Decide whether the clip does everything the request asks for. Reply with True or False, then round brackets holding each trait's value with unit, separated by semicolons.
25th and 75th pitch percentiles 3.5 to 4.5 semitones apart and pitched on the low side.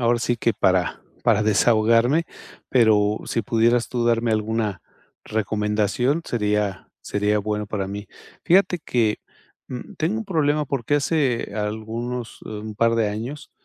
False (2.7 semitones; 115 Hz)